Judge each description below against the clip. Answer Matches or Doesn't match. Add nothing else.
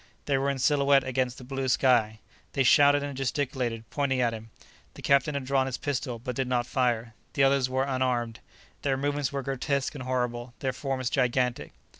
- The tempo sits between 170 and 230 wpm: Matches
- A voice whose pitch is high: Doesn't match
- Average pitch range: Doesn't match